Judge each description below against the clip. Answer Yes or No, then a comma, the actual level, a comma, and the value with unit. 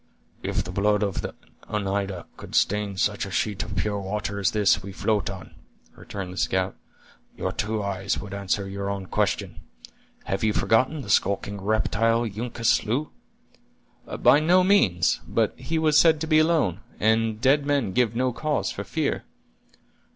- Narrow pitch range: No, average, 3.9 semitones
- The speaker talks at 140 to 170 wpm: Yes, average, 165 wpm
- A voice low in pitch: Yes, low, 105 Hz